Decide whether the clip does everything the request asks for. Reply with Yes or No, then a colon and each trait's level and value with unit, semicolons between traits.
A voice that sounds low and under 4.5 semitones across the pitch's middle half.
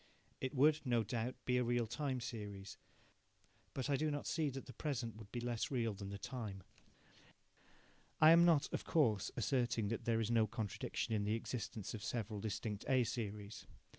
Yes: low, 115 Hz; average, 3.6 semitones